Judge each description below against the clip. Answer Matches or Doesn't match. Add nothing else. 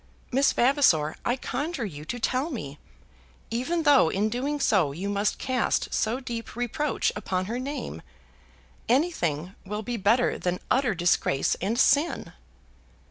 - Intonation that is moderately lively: Doesn't match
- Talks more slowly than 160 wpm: Matches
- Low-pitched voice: Doesn't match